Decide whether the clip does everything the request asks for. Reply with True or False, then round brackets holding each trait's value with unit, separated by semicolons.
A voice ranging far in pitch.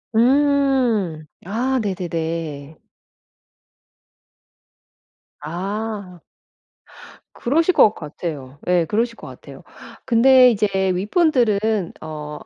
True (6.8 semitones)